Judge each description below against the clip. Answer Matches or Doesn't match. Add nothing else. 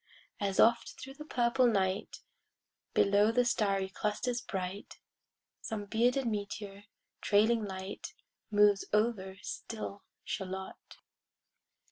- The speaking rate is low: Matches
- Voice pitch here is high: Matches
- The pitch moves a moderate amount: Matches